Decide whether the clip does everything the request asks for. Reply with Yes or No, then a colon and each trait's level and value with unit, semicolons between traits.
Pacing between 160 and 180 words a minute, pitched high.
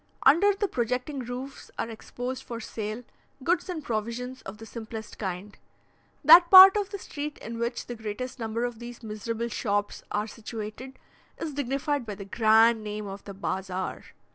Yes: average, 165 wpm; high, 235 Hz